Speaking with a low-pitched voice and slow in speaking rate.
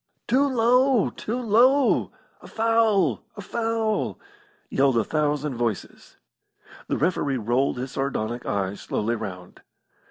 No: medium, 150 Hz; slow, 120 wpm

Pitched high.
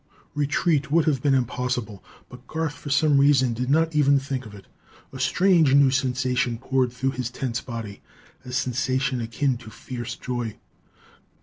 No: low, 130 Hz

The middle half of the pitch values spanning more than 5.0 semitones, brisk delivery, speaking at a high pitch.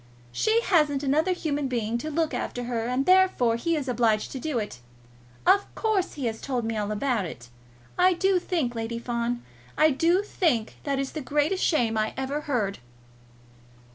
No: wide, 5.5 semitones; average, 180 wpm; very high, 270 Hz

